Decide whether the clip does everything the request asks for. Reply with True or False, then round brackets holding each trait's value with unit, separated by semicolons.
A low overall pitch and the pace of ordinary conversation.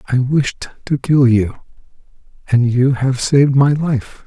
True (130 Hz; 155 wpm)